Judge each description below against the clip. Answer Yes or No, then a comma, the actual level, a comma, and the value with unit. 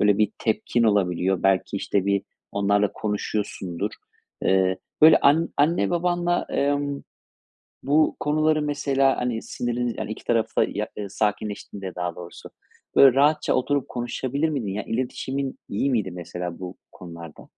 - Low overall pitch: Yes, low, 110 Hz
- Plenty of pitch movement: Yes, wide, 6.3 semitones